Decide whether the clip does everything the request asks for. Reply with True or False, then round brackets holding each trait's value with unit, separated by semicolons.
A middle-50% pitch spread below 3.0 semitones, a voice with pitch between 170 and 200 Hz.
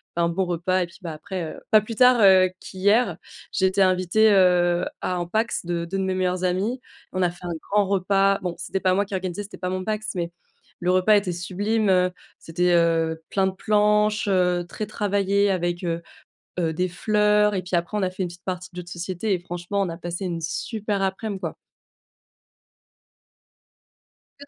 True (2.5 semitones; 185 Hz)